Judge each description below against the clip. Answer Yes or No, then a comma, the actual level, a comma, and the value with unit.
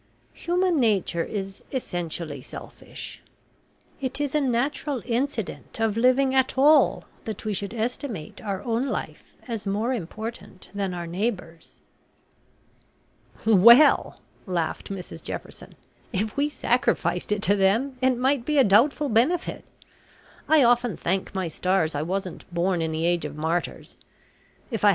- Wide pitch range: Yes, wide, 6.1 semitones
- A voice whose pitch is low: No, high, 215 Hz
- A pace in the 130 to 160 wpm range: Yes, average, 140 wpm